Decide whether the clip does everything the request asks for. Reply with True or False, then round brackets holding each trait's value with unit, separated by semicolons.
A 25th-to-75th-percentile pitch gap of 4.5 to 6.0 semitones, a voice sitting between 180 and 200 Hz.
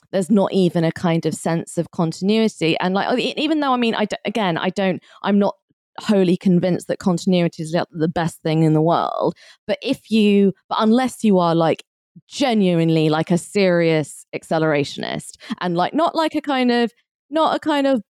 True (5.1 semitones; 190 Hz)